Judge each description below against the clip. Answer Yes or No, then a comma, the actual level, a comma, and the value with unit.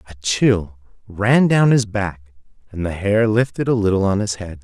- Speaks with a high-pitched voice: No, low, 100 Hz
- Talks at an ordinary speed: Yes, average, 195 wpm